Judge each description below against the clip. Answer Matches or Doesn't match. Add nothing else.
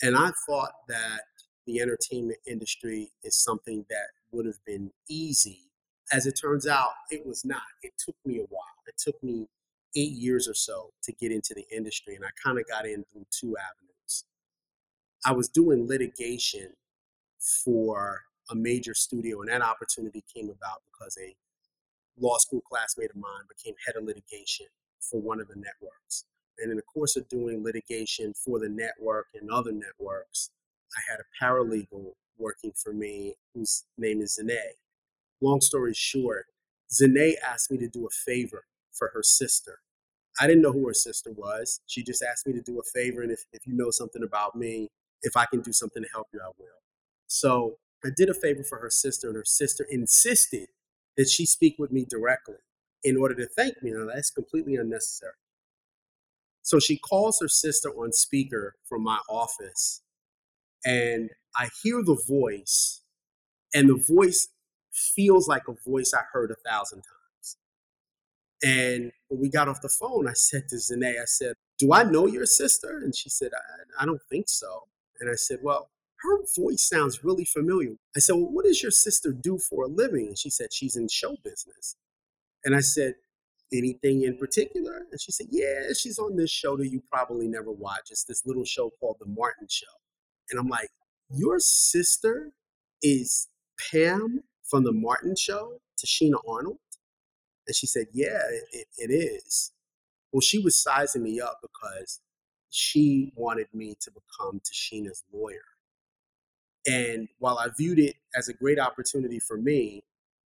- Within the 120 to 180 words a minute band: Matches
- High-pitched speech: Doesn't match